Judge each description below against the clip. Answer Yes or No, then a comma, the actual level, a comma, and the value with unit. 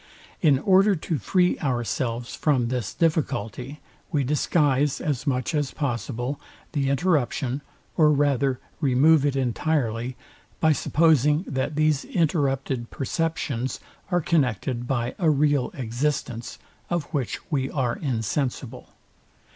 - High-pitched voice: No, medium, 140 Hz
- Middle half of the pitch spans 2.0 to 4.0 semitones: Yes, average, 3.5 semitones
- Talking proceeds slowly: Yes, slow, 115 wpm